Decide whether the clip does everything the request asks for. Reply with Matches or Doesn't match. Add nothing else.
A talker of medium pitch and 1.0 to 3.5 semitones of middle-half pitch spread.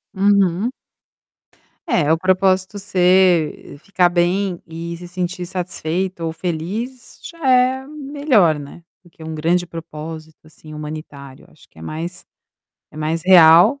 Matches